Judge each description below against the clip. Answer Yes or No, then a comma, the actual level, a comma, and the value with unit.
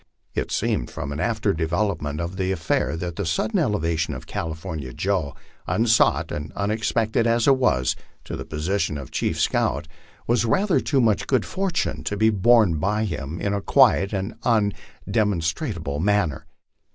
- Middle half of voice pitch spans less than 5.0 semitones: No, wide, 5.5 semitones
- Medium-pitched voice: No, low, 100 Hz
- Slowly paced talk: No, average, 160 wpm